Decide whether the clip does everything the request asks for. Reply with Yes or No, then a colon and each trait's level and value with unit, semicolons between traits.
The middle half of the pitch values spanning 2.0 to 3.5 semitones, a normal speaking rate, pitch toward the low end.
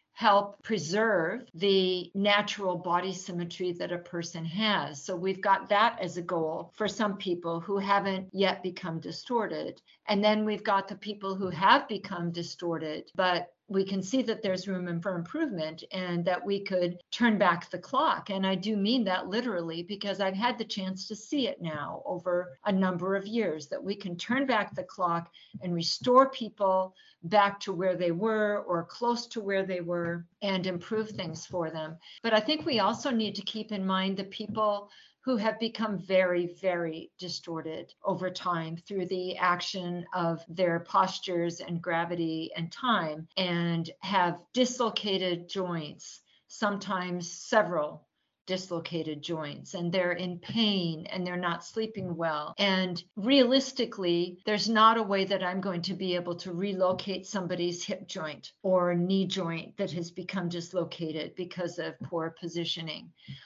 No: average, 2.9 semitones; average, 165 wpm; medium, 185 Hz